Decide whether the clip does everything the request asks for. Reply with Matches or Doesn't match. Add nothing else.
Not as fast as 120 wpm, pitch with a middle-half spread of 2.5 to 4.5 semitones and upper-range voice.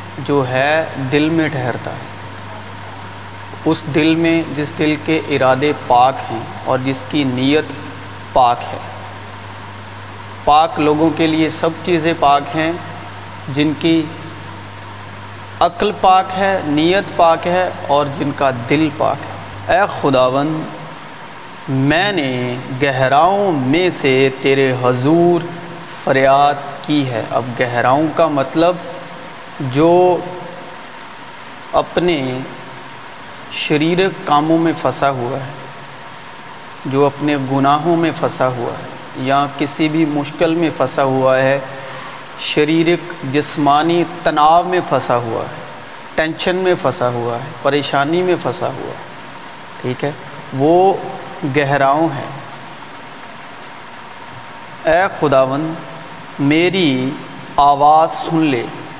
Doesn't match